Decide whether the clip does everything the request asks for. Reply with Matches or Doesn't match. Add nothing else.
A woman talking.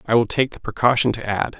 Doesn't match